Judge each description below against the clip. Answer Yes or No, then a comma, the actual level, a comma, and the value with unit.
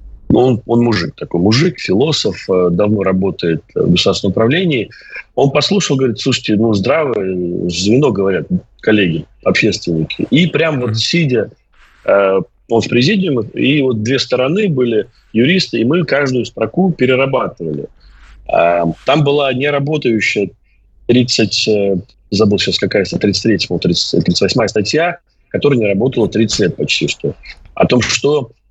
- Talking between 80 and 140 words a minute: Yes, average, 125 wpm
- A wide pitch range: Yes, wide, 5.7 semitones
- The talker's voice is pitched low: Yes, low, 115 Hz